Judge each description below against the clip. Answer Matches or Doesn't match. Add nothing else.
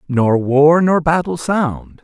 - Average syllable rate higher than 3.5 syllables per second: Doesn't match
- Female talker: Doesn't match